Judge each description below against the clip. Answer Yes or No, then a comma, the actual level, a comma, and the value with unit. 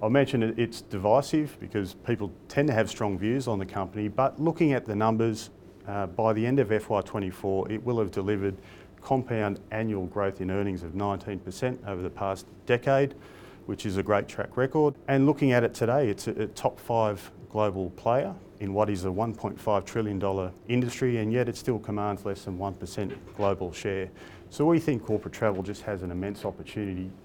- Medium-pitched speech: No, low, 105 Hz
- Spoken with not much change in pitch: No, average, 3.3 semitones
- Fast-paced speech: No, average, 185 wpm